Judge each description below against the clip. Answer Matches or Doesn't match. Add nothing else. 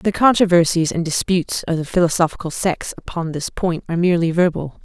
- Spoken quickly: Doesn't match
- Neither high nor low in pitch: Matches